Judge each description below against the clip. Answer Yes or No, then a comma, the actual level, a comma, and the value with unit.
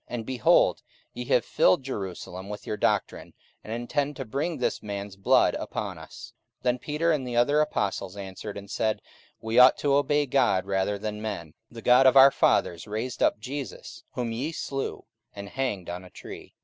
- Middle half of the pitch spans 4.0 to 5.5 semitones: Yes, average, 5.0 semitones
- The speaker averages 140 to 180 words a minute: No, average, 190 wpm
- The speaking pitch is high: No, low, 115 Hz